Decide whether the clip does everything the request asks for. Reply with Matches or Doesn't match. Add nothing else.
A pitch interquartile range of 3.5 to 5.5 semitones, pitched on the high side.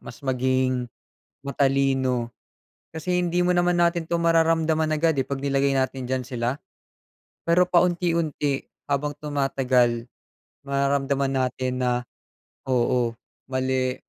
Doesn't match